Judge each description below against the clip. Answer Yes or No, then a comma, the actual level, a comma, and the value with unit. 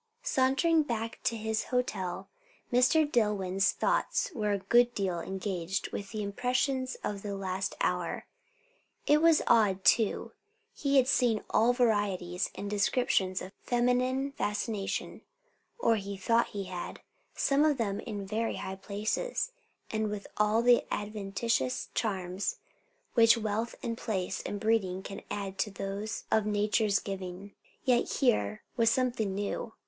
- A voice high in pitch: Yes, high, 210 Hz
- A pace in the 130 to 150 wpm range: Yes, average, 140 wpm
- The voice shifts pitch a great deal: No, average, 3.6 semitones